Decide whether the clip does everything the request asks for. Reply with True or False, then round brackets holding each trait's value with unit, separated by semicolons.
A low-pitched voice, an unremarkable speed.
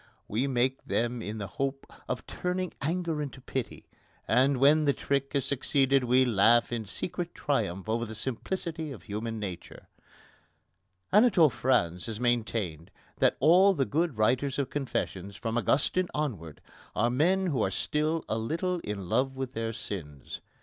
True (130 Hz; 155 wpm)